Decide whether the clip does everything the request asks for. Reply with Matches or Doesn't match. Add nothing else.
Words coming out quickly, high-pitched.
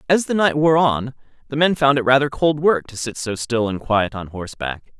Doesn't match